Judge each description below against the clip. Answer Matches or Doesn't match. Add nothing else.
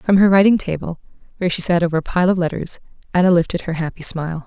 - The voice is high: Doesn't match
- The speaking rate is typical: Doesn't match